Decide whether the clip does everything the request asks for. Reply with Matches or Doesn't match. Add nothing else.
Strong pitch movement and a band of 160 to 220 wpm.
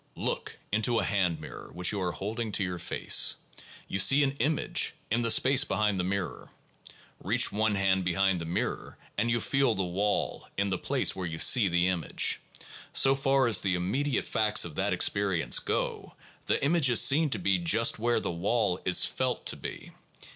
Doesn't match